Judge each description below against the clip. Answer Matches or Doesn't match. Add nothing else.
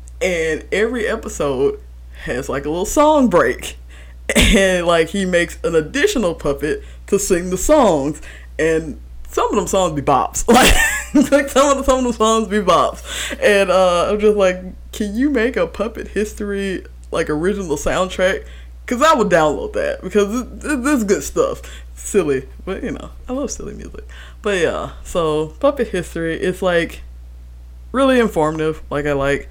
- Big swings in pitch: Matches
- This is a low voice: Doesn't match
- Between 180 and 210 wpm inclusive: Doesn't match